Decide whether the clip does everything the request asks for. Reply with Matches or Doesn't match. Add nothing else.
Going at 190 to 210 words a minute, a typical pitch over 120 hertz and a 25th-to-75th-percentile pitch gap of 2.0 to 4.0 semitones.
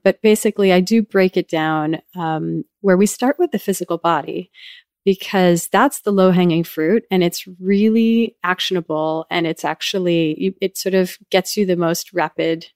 Doesn't match